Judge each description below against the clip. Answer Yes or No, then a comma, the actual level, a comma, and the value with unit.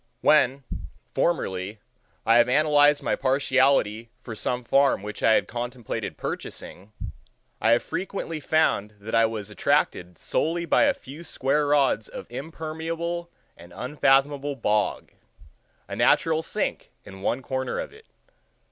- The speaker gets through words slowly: Yes, slow, 130 wpm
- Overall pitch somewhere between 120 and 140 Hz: Yes, low, 135 Hz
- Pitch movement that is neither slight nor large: No, wide, 5.7 semitones